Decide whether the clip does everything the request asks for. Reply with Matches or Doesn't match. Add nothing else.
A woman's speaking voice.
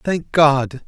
Doesn't match